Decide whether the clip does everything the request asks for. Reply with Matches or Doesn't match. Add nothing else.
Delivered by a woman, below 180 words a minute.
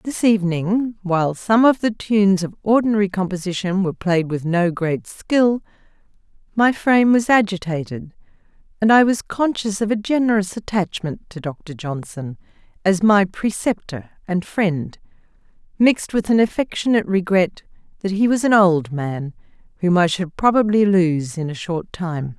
Matches